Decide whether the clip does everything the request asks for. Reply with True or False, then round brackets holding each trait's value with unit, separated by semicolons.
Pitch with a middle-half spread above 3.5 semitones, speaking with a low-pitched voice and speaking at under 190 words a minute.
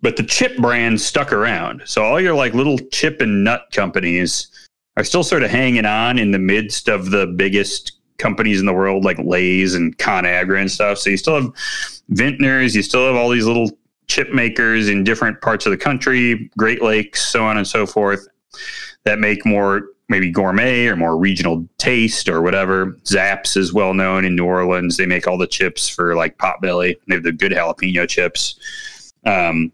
False (3.9 semitones; 100 Hz; 195 wpm)